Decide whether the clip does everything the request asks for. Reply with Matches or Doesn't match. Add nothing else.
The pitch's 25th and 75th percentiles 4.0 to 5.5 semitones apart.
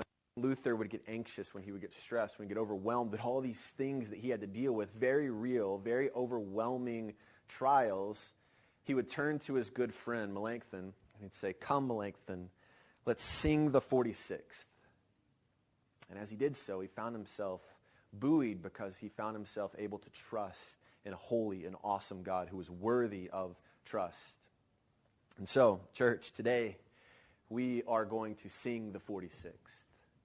Doesn't match